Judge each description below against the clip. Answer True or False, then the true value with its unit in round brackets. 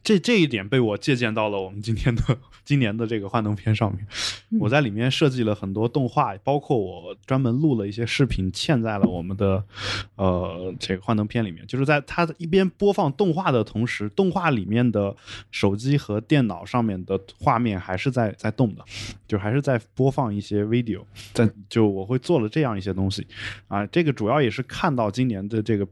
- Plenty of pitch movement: False (4.9 semitones)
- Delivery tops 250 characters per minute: True (310 characters per minute)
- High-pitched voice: False (115 Hz)